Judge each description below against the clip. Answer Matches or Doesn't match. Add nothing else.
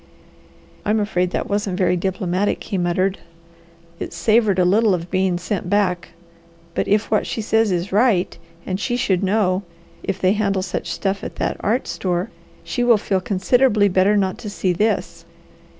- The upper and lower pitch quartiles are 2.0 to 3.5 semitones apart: Matches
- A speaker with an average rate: Matches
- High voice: Matches